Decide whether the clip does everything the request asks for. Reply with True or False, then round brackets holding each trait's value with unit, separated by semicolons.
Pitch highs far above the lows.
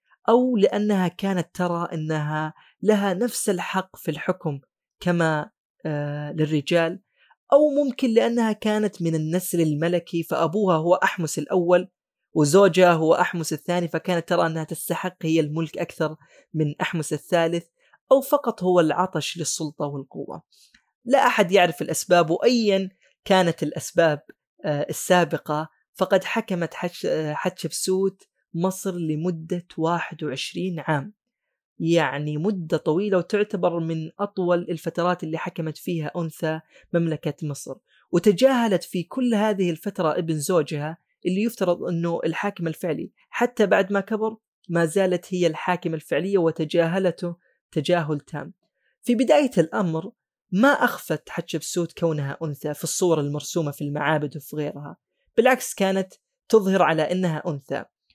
False (3.3 semitones)